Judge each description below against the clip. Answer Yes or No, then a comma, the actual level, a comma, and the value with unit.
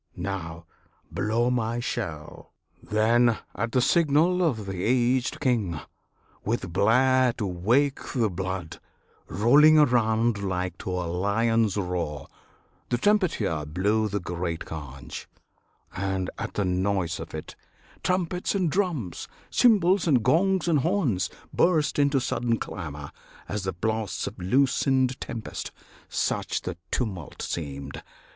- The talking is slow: Yes, slow, 125 wpm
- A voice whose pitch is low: Yes, low, 110 Hz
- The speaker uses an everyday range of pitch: No, wide, 6.4 semitones